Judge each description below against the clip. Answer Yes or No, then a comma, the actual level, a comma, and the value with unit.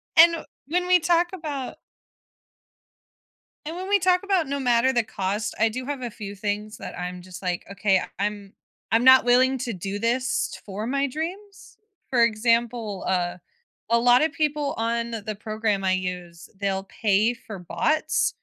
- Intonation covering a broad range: Yes, wide, 5.7 semitones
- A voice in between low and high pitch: No, high, 235 Hz